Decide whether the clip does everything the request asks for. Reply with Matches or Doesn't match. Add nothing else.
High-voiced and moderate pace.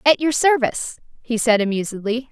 Matches